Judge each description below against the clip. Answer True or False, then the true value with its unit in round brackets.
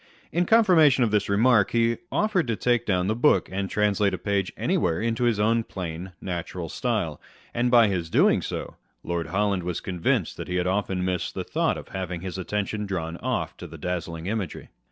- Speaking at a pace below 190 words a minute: False (195 wpm)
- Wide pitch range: False (4.4 semitones)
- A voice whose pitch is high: False (100 Hz)